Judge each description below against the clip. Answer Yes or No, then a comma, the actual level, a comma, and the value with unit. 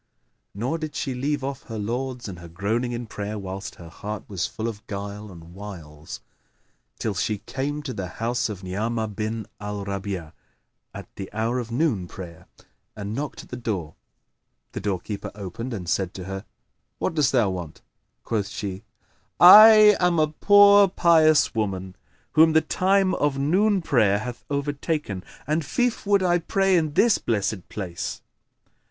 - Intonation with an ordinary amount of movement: No, wide, 7.2 semitones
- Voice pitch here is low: Yes, low, 115 Hz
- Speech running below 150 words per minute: No, average, 165 wpm